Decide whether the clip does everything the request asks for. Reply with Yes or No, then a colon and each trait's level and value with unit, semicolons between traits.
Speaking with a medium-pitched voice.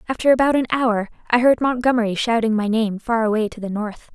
No: high, 230 Hz